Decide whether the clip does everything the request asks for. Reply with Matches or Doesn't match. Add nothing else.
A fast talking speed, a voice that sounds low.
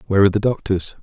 Matches